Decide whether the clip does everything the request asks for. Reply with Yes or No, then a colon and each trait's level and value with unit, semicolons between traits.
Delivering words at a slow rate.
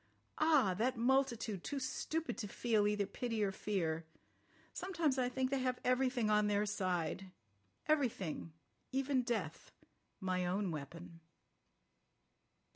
Yes: slow, 115 wpm